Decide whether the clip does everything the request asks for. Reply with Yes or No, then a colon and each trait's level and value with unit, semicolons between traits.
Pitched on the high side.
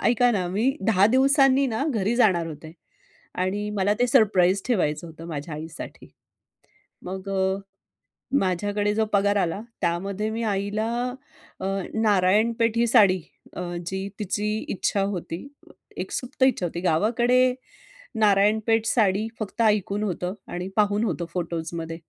Yes: high, 205 Hz